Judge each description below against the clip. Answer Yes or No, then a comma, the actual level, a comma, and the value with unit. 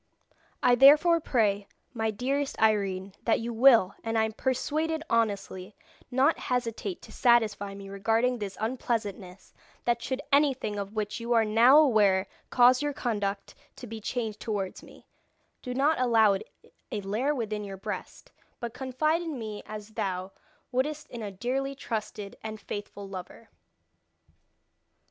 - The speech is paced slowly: No, average, 150 wpm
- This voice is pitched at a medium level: No, high, 225 Hz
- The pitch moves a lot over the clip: No, average, 4.0 semitones